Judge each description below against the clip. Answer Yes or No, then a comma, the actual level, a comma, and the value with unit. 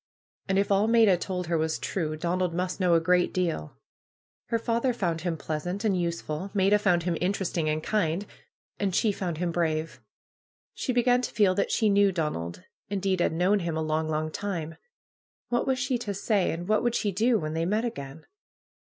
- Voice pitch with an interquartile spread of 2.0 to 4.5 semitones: Yes, average, 4.0 semitones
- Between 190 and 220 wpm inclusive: Yes, average, 195 wpm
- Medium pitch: Yes, medium, 180 Hz